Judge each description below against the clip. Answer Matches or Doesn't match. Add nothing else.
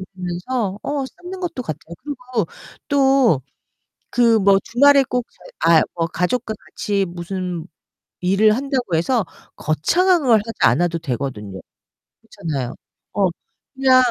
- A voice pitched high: Matches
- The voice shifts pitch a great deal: Matches